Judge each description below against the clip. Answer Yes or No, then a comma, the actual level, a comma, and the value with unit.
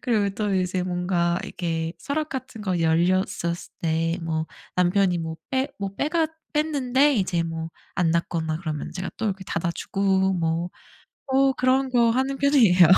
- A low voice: No, medium, 185 Hz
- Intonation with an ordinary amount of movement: No, wide, 6.8 semitones